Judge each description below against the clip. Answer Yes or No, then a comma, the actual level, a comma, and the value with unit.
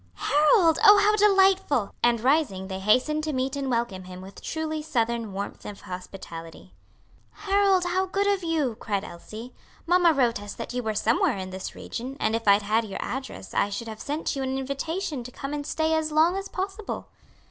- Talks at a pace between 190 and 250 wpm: Yes, average, 195 wpm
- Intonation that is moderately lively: No, wide, 7.2 semitones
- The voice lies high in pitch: Yes, very high, 265 Hz